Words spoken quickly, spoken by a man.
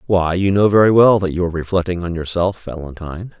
Yes: fast, 210 wpm; male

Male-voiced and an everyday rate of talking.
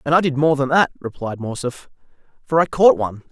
No: male; fast, 215 wpm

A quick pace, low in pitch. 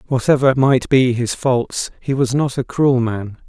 No: average, 190 wpm; low, 130 Hz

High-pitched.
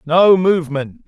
No: medium, 170 Hz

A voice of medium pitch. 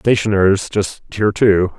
No: low, 100 Hz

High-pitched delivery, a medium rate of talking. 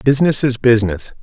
No: low, 120 Hz; average, 145 wpm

